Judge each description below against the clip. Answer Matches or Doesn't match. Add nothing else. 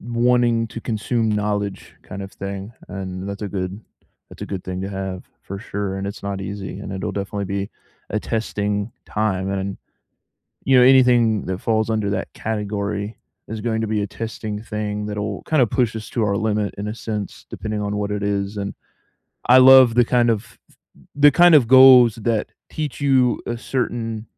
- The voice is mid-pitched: Doesn't match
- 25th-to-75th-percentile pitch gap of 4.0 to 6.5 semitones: Doesn't match